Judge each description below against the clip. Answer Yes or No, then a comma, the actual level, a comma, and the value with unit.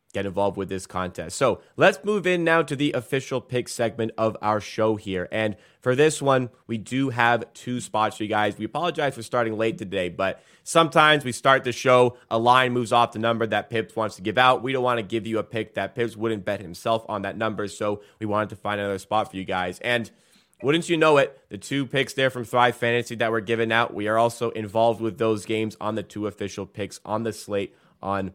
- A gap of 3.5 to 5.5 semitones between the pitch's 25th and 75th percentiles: No, average, 2.9 semitones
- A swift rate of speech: Yes, fast, 240 wpm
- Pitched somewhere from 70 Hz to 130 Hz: Yes, low, 115 Hz